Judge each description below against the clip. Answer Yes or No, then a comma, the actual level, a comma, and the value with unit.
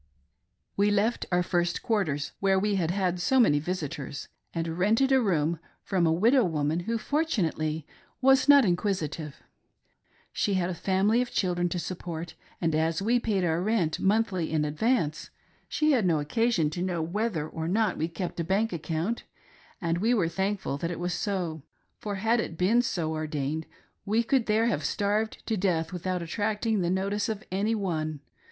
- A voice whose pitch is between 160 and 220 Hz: Yes, medium, 185 Hz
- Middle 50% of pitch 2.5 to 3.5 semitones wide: No, average, 4.8 semitones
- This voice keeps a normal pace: Yes, average, 175 wpm